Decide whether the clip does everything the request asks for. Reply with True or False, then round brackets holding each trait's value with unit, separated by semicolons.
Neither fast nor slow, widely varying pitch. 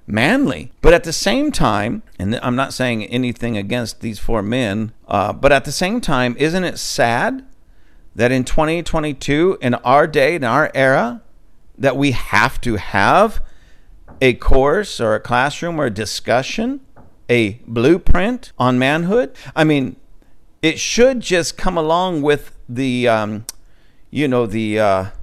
True (150 wpm; 5.8 semitones)